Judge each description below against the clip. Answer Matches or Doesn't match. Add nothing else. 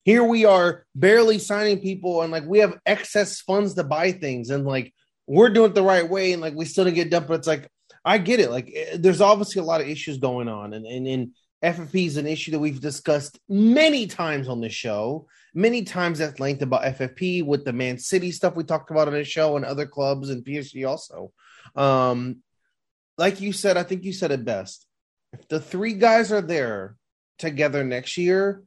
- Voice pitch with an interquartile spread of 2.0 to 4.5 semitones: Doesn't match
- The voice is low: Doesn't match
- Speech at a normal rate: Doesn't match